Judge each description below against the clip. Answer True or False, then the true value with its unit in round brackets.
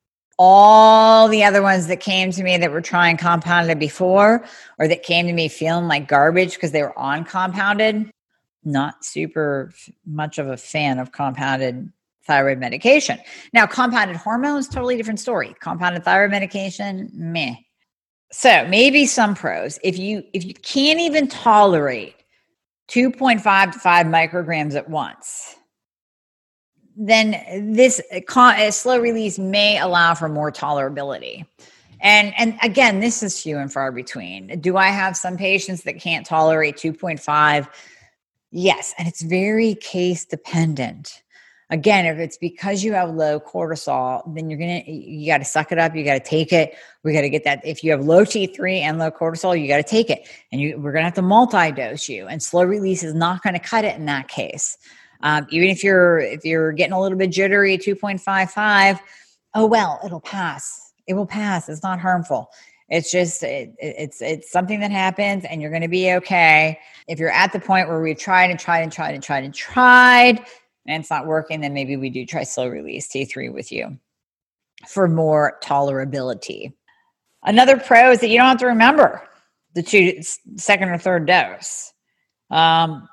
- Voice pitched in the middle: True (180 Hz)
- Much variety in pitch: False (4.6 semitones)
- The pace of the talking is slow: False (180 wpm)